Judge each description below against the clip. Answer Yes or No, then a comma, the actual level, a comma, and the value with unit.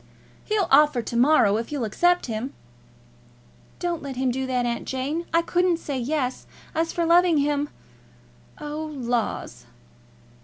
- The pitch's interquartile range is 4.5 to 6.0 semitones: Yes, average, 5.0 semitones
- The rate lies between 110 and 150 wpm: Yes, average, 145 wpm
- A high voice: Yes, very high, 290 Hz